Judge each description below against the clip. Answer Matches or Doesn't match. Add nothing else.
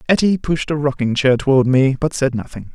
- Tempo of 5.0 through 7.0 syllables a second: Matches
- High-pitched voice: Doesn't match